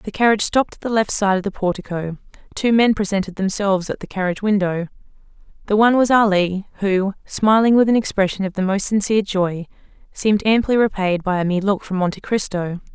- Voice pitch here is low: No, high, 200 Hz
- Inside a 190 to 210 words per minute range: Yes, average, 195 wpm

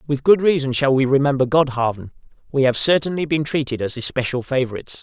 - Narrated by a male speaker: Yes, male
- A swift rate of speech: No, average, 180 wpm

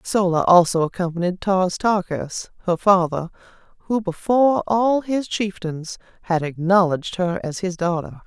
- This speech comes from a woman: Yes, female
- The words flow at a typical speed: No, slow, 130 wpm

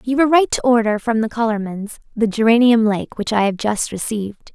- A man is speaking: No, female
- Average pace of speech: No, fast, 210 wpm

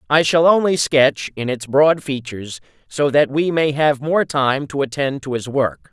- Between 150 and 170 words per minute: No, fast, 205 wpm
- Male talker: Yes, male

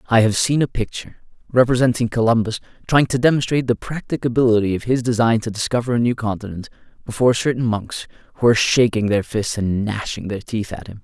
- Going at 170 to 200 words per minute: Yes, average, 185 wpm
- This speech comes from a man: Yes, male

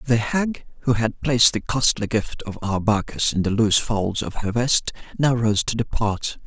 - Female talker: No, male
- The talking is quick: No, average, 195 wpm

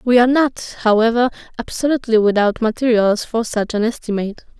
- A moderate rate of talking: Yes, average, 145 wpm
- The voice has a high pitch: Yes, high, 230 Hz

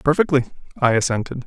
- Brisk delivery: No, slow, 125 wpm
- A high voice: No, low, 135 Hz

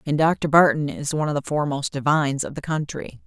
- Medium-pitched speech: Yes, medium, 150 Hz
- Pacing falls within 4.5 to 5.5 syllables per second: No, 6.1 syllables/s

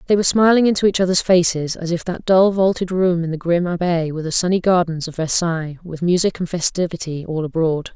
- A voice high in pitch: No, medium, 175 Hz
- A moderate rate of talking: No, fast, 220 wpm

